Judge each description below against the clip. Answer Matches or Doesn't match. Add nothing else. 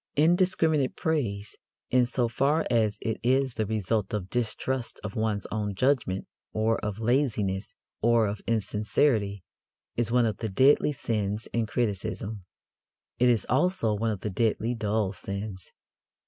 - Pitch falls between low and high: Doesn't match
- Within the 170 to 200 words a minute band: Doesn't match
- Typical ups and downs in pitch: Matches